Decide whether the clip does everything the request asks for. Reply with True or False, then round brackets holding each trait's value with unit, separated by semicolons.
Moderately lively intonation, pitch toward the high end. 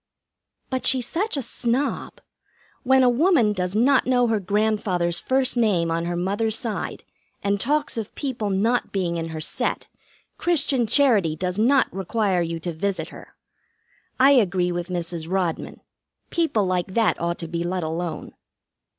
False (6.0 semitones; 205 Hz)